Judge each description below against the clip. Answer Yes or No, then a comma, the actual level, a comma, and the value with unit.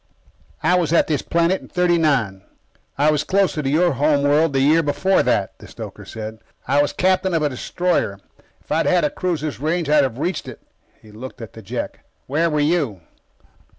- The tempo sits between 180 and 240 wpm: Yes, average, 200 wpm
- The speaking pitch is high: No, medium, 150 Hz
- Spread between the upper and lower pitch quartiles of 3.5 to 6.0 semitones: Yes, average, 4.0 semitones